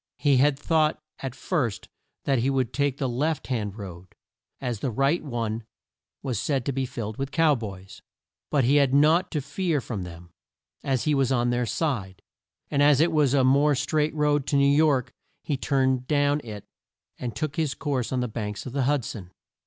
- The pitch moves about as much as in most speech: Yes, average, 3.5 semitones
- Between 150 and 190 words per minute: No, average, 200 wpm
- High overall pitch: No, low, 135 Hz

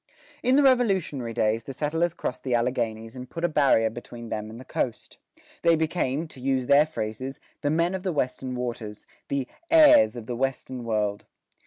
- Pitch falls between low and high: No, low, 130 Hz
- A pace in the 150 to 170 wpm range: No, average, 185 wpm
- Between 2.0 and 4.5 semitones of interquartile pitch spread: No, wide, 5.5 semitones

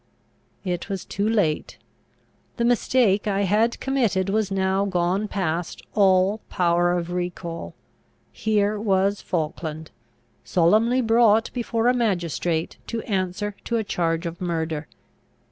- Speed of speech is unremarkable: No, slow, 125 wpm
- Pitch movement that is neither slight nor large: Yes, average, 3.8 semitones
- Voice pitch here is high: Yes, high, 195 Hz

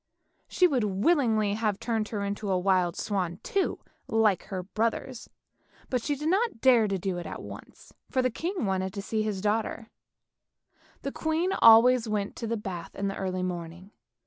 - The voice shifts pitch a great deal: No, average, 4.4 semitones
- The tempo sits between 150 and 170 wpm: No, average, 180 wpm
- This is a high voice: Yes, high, 215 Hz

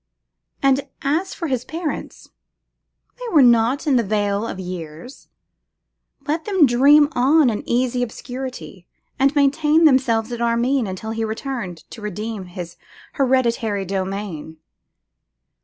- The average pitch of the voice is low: No, high, 240 Hz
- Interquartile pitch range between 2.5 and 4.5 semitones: No, average, 5.0 semitones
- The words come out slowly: Yes, slow, 125 wpm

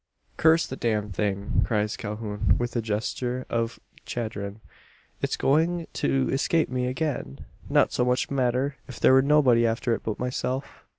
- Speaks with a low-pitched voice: Yes, low, 125 Hz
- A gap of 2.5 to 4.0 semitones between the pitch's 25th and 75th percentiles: Yes, average, 3.7 semitones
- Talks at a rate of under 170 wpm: Yes, average, 160 wpm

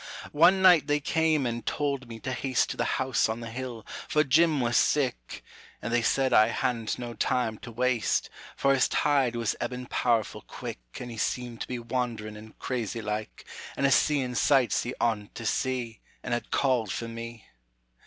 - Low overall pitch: Yes, low, 125 Hz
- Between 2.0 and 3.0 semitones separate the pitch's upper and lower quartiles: Yes, average, 2.7 semitones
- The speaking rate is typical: Yes, average, 190 wpm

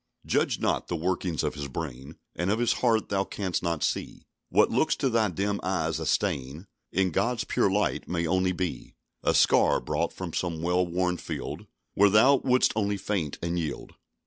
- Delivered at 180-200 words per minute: Yes, average, 190 wpm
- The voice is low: Yes, very low, 90 Hz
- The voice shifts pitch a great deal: No, average, 3.4 semitones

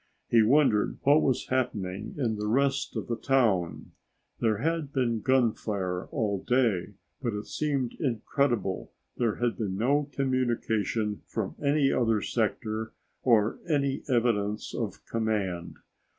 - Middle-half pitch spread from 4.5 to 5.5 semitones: No, average, 4.1 semitones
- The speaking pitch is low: Yes, low, 115 Hz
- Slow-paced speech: Yes, slow, 130 wpm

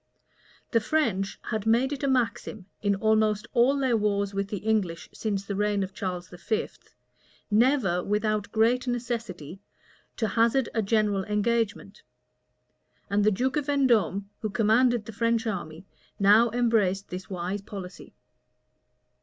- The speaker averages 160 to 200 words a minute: No, average, 140 wpm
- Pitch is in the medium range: No, high, 215 Hz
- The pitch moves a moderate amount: Yes, average, 3.0 semitones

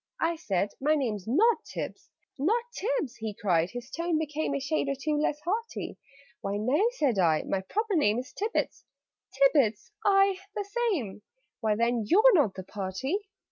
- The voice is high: Yes, very high, 275 Hz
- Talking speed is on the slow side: No, average, 175 wpm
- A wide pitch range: Yes, wide, 8.8 semitones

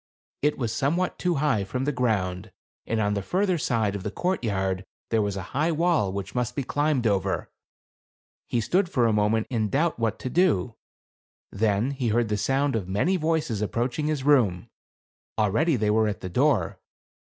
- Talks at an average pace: Yes, average, 185 wpm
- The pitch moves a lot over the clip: Yes, wide, 6.1 semitones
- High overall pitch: No, low, 115 Hz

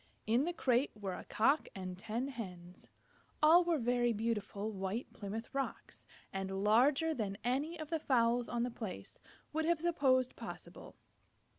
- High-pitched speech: Yes, high, 240 Hz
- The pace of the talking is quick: No, average, 155 wpm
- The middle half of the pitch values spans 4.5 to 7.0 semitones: Yes, wide, 5.4 semitones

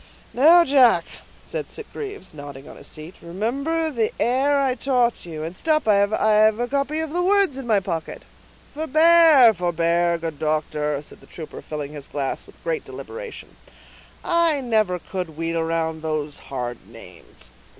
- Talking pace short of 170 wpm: Yes, average, 155 wpm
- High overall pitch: Yes, high, 210 Hz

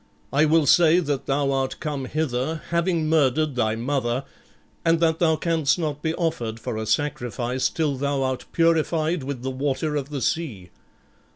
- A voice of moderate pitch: Yes, medium, 145 Hz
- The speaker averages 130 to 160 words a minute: No, average, 170 wpm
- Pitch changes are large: No, average, 3.5 semitones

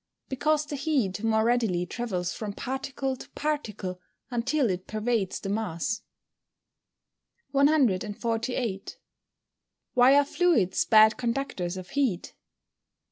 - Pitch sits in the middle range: No, high, 230 Hz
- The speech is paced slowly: Yes, slow, 110 wpm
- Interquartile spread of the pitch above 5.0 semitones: Yes, wide, 5.6 semitones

